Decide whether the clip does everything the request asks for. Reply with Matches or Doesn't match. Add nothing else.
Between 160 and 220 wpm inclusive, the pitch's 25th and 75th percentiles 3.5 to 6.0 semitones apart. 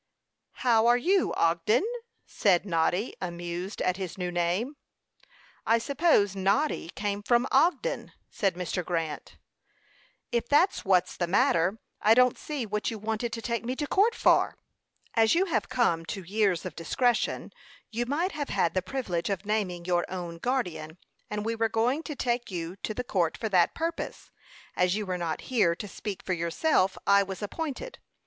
Matches